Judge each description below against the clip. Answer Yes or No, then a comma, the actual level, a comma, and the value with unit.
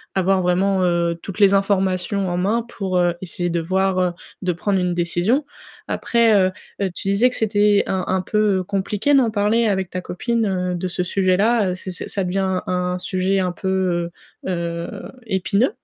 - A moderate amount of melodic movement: No, narrow, 2.1 semitones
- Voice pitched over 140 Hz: Yes, high, 190 Hz